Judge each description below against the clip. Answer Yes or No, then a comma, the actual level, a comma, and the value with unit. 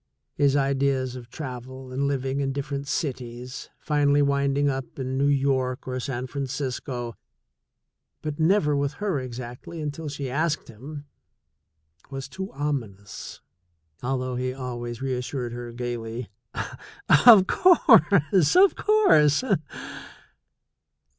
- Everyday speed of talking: No, slow, 115 wpm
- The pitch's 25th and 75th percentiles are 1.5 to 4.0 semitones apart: Yes, narrow, 2.5 semitones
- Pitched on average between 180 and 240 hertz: No, low, 135 Hz